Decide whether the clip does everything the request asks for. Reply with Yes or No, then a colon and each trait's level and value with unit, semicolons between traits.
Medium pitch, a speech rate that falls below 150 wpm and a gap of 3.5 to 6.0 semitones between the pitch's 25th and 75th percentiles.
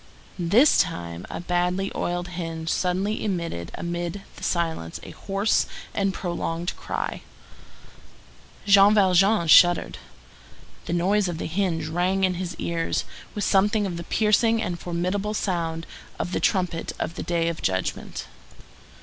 No: medium, 175 Hz; average, 140 wpm; average, 2.7 semitones